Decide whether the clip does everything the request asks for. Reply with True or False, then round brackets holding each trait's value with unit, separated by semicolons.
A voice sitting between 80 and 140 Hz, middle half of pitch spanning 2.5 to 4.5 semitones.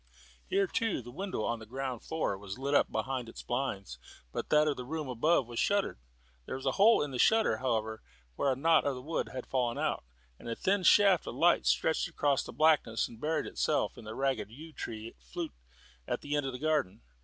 False (135 Hz; 5.3 semitones)